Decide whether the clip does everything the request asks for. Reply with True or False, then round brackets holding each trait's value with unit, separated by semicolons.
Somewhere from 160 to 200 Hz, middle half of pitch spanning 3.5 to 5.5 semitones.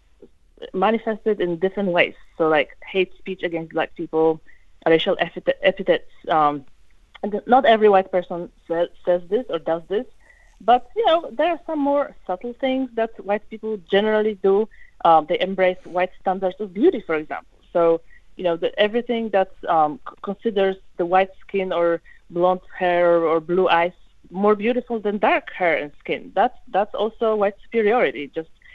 True (190 Hz; 4.3 semitones)